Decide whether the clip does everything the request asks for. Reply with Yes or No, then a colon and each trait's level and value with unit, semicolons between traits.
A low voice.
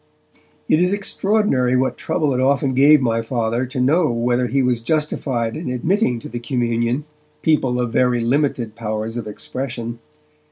Yes: low, 125 Hz